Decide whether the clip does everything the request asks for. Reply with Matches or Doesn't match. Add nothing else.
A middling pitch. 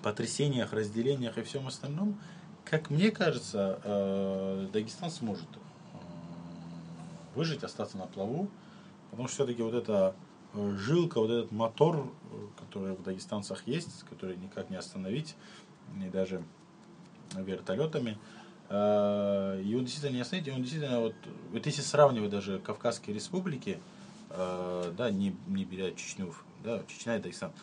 Doesn't match